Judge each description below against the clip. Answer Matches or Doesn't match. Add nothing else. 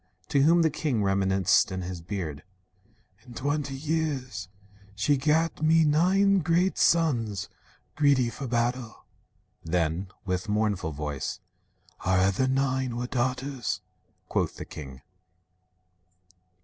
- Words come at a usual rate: Doesn't match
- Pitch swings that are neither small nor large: Doesn't match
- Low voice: Matches